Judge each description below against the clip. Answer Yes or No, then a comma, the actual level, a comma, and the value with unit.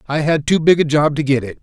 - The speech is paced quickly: Yes, fast, 330 wpm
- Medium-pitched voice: Yes, medium, 150 Hz